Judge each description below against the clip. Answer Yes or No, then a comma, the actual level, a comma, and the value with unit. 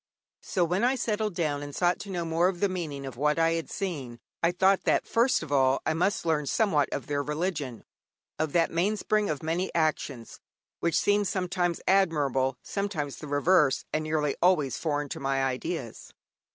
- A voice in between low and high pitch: Yes, medium, 165 Hz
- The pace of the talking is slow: No, average, 185 wpm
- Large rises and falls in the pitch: No, average, 4.5 semitones